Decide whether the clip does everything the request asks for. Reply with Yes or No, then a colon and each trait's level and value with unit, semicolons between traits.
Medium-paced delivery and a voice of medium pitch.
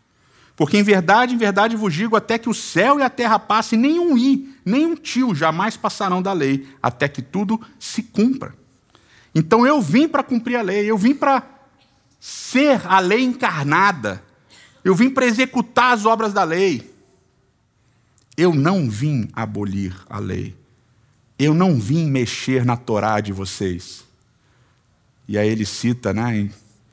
Yes: average, 155 wpm; medium, 160 Hz